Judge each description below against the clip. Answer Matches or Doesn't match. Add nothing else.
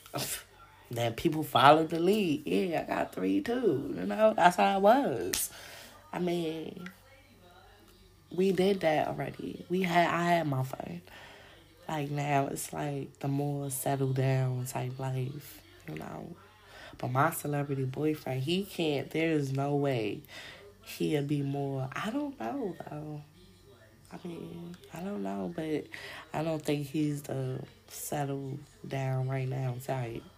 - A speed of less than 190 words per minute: Matches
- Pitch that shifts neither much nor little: Matches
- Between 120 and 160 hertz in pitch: Matches